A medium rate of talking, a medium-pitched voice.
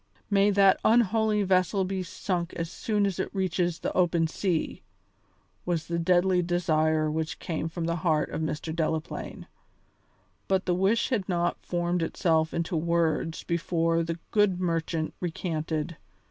Yes: average, 145 wpm; medium, 170 Hz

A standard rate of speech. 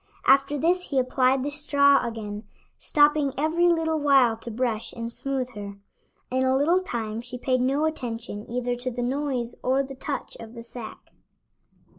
Yes: average, 170 wpm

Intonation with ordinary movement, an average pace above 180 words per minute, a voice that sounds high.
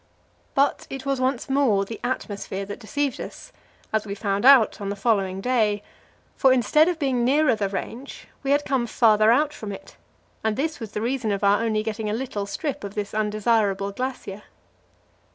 Yes: average, 4.5 semitones; average, 190 wpm; high, 225 Hz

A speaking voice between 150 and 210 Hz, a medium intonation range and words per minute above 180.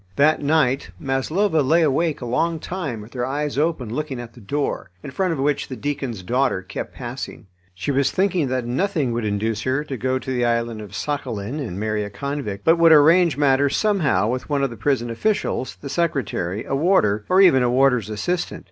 No: low, 135 Hz; average, 4.6 semitones; fast, 205 wpm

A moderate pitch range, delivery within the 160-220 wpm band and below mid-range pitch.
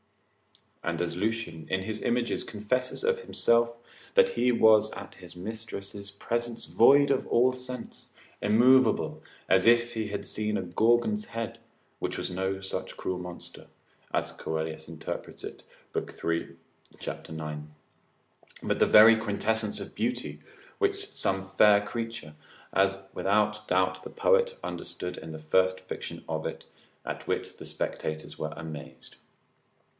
No: average, 4.7 semitones; average, 140 wpm; low, 105 Hz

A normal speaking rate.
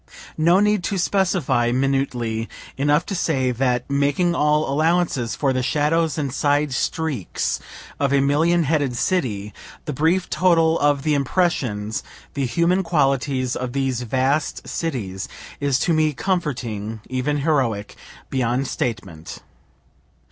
No: slow, 130 wpm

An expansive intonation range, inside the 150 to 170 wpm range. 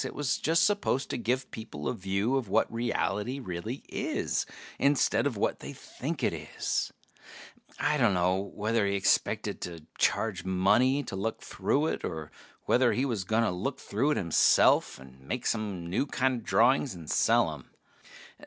Yes: wide, 5.7 semitones; average, 165 wpm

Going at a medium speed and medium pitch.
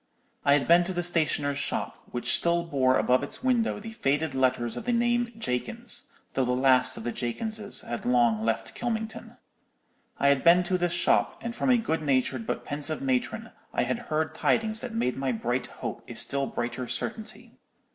Yes: average, 190 wpm; medium, 150 Hz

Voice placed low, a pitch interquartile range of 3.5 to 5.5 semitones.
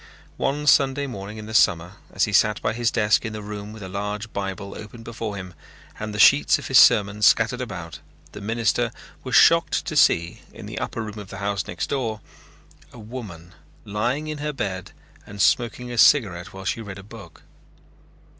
No: low, 105 Hz; average, 3.0 semitones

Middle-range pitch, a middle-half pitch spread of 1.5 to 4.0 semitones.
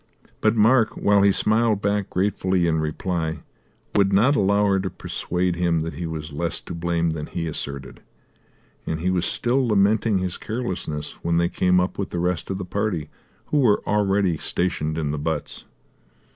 No: very low, 90 Hz; average, 3.7 semitones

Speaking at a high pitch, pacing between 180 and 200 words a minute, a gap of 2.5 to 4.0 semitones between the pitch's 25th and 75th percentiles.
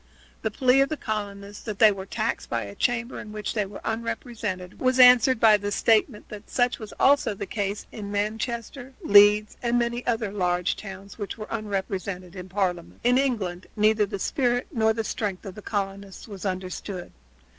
Yes: high, 210 Hz; average, 185 wpm; average, 3.0 semitones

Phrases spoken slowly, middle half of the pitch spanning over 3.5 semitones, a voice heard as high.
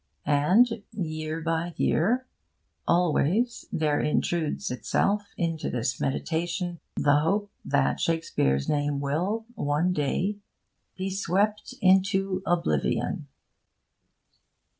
No: slow, 95 wpm; average, 4.6 semitones; medium, 170 Hz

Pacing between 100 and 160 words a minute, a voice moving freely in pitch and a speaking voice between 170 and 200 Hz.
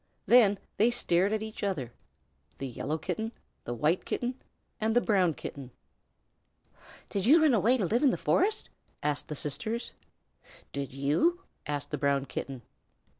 Yes: average, 155 wpm; wide, 8.6 semitones; high, 190 Hz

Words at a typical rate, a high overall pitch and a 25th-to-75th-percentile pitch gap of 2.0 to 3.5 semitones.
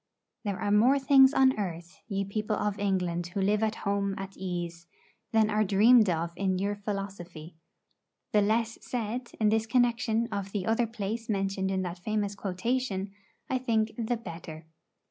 Yes: average, 165 wpm; high, 205 Hz; average, 2.8 semitones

